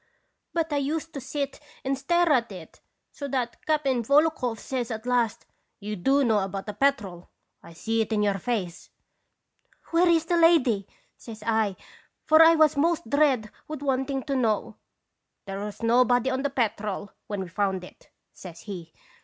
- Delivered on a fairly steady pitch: No, wide, 5.4 semitones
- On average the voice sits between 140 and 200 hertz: No, high, 245 Hz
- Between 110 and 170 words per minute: No, average, 185 wpm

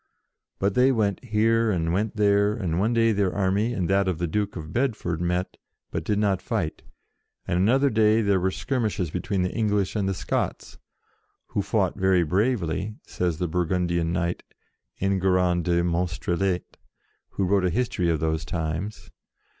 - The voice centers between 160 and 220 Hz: No, very low, 95 Hz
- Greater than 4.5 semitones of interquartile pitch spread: No, average, 3.3 semitones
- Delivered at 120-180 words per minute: Yes, average, 170 wpm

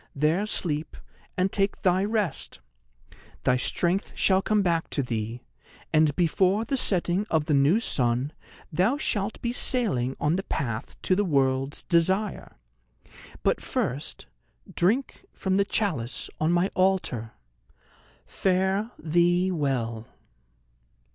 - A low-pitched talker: No, medium, 175 Hz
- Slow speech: Yes, slow, 125 wpm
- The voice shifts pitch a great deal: Yes, wide, 5.8 semitones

